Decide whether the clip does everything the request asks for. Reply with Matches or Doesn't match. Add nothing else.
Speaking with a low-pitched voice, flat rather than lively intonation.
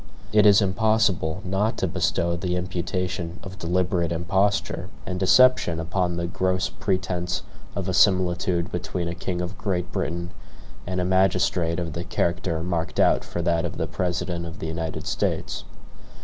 Matches